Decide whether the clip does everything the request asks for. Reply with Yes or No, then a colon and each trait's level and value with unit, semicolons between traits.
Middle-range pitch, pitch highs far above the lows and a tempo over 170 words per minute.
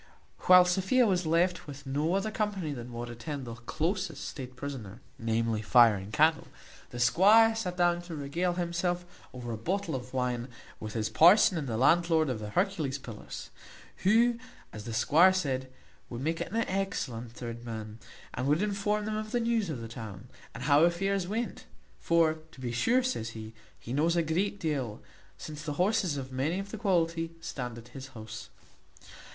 Yes: medium, 155 Hz; wide, 7.3 semitones; average, 180 wpm